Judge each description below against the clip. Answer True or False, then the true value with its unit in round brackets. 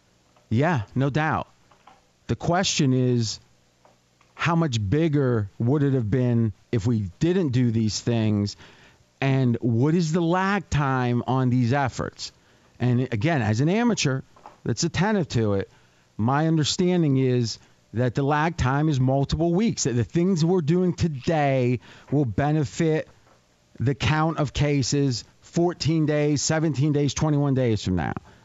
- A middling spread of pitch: True (5.0 semitones)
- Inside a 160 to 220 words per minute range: False (140 wpm)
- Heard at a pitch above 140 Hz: False (135 Hz)